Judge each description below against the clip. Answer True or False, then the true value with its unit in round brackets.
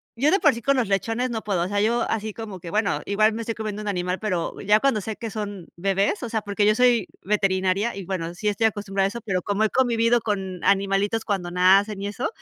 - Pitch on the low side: False (205 Hz)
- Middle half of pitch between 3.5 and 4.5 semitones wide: False (2.5 semitones)